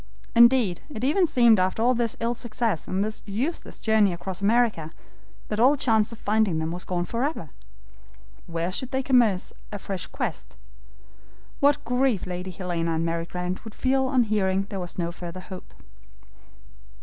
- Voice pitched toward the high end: Yes, high, 210 Hz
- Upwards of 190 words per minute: No, average, 160 wpm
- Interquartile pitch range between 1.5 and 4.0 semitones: No, average, 5.1 semitones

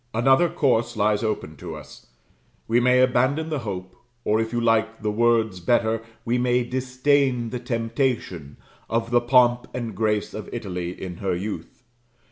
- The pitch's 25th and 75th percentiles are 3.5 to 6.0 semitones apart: No, average, 2.8 semitones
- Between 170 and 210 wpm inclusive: No, average, 160 wpm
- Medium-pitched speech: No, low, 115 Hz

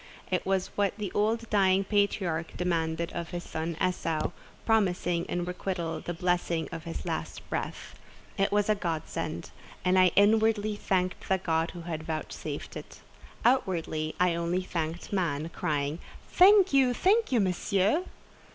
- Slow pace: No, average, 150 wpm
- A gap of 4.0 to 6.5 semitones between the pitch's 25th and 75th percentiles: No, average, 3.5 semitones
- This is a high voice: No, medium, 180 Hz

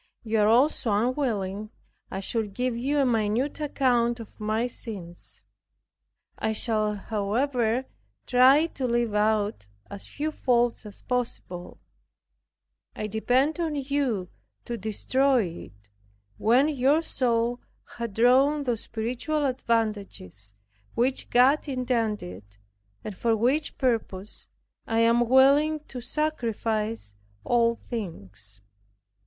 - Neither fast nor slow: No, slow, 115 wpm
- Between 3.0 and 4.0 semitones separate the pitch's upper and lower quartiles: Yes, average, 3.6 semitones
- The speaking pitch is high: Yes, high, 235 Hz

